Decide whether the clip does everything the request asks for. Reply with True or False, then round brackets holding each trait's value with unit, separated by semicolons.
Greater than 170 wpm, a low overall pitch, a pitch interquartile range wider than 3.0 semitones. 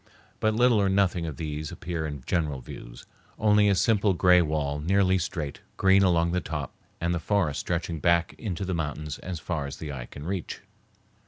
True (190 wpm; 85 Hz; 4.0 semitones)